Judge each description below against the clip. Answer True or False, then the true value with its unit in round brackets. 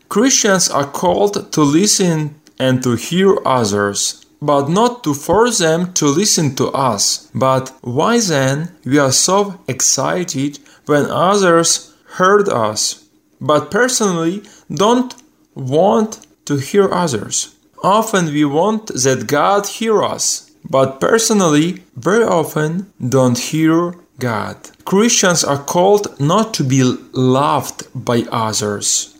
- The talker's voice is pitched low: False (160 Hz)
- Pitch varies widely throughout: True (6.9 semitones)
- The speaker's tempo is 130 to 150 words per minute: False (120 wpm)